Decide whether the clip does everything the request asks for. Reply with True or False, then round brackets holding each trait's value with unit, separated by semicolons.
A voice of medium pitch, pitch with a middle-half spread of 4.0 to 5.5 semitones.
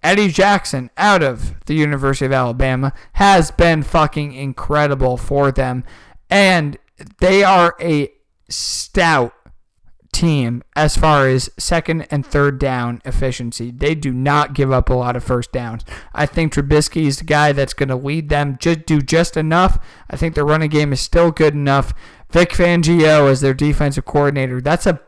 False (145 Hz; 3.2 semitones)